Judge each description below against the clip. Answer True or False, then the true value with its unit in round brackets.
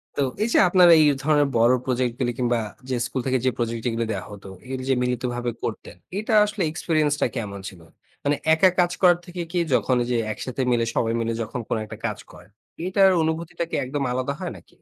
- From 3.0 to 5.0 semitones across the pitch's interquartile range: False (5.5 semitones)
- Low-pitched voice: True (130 Hz)